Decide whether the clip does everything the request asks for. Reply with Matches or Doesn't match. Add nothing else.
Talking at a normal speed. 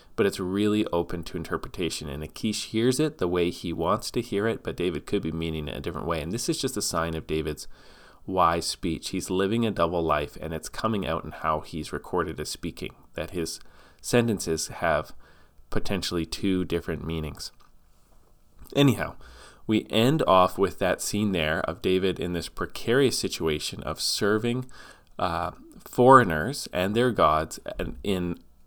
Matches